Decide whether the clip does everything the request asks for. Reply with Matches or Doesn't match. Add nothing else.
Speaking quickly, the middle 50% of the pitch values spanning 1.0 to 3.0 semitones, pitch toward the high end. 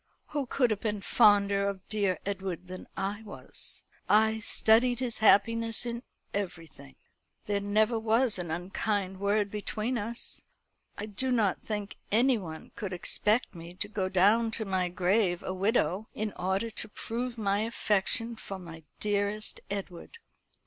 Doesn't match